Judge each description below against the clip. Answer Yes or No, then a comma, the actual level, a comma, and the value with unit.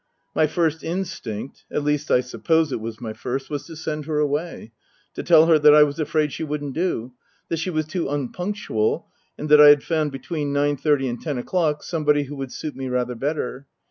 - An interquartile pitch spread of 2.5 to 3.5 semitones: Yes, average, 2.9 semitones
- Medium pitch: Yes, medium, 150 Hz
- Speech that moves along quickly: Yes, fast, 210 wpm